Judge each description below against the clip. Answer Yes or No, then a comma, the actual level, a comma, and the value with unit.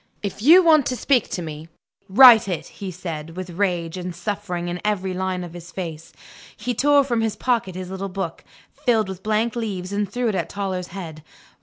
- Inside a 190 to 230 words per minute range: Yes, average, 200 wpm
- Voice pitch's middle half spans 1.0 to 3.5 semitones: No, average, 3.9 semitones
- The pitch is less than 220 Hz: Yes, high, 190 Hz